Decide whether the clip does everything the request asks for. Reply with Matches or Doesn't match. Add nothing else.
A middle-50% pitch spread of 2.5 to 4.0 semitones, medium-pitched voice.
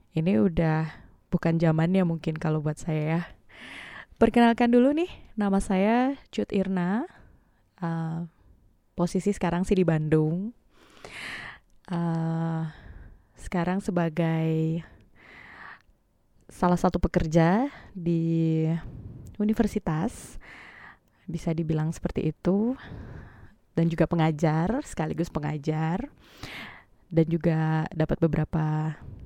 Matches